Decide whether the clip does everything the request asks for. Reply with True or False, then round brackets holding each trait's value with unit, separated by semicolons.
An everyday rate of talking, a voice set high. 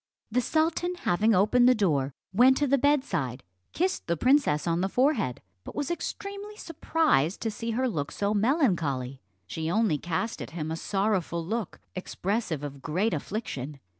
True (165 wpm; 205 Hz)